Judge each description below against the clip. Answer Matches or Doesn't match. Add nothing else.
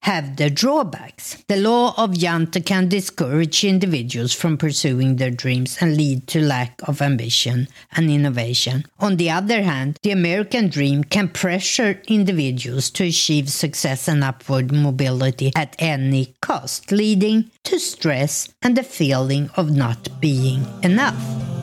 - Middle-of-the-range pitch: Matches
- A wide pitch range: Matches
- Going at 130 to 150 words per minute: Matches